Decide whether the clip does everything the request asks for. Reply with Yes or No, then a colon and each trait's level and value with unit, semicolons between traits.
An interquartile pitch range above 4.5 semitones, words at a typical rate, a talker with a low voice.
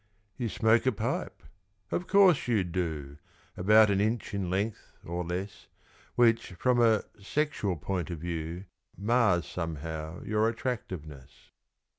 No: average, 5.0 semitones; slow, 130 wpm; low, 100 Hz